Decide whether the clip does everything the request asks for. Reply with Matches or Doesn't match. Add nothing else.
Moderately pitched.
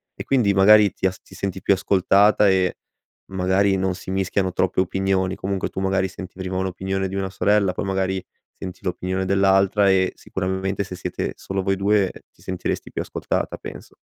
Doesn't match